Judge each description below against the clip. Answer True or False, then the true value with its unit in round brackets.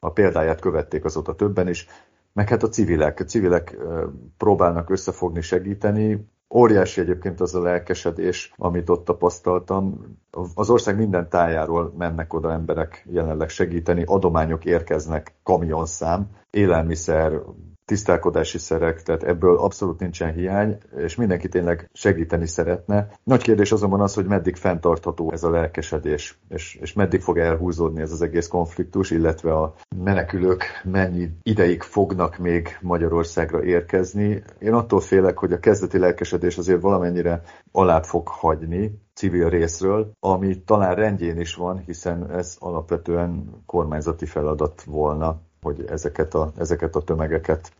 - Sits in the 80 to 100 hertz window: True (90 Hz)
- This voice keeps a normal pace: True (135 wpm)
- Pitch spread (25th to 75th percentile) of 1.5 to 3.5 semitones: True (2.4 semitones)